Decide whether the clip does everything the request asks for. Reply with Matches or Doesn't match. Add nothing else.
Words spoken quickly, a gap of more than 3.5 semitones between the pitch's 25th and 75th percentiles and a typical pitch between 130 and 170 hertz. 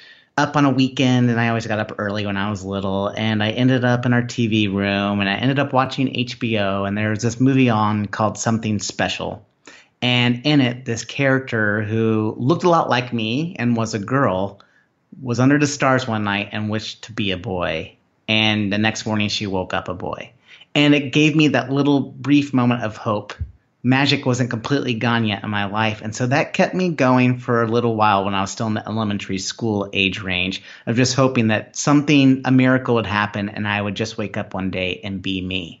Doesn't match